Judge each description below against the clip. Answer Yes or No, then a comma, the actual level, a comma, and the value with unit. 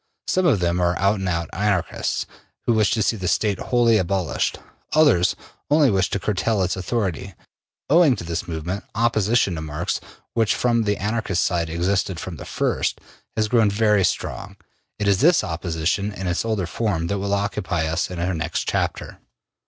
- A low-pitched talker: Yes, low, 100 Hz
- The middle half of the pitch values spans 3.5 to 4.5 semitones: Yes, average, 3.9 semitones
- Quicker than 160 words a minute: Yes, average, 180 wpm